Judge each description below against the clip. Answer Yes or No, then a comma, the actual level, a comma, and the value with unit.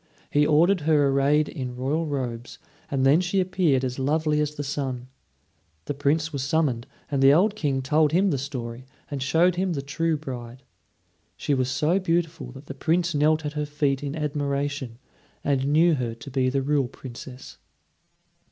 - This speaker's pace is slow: No, average, 180 wpm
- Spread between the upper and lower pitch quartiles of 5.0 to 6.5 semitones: No, average, 3.0 semitones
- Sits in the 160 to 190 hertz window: No, medium, 145 Hz